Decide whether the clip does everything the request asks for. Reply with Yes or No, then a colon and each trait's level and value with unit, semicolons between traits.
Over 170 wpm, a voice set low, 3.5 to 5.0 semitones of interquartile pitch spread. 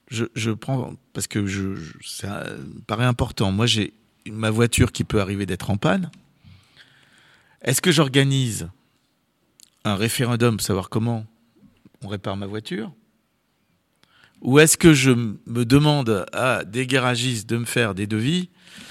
No: average, 150 wpm; low, 120 Hz; average, 4.1 semitones